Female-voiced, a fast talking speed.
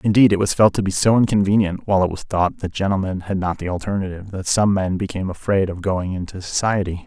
No: male; fast, 230 wpm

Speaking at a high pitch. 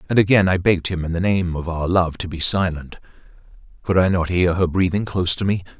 No: very low, 90 Hz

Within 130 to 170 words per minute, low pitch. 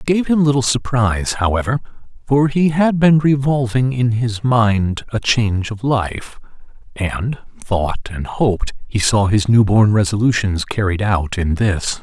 Yes: average, 160 wpm; low, 115 Hz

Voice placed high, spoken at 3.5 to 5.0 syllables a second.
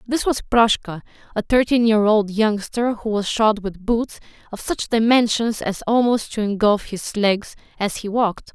Yes: high, 220 Hz; 4.5 syllables/s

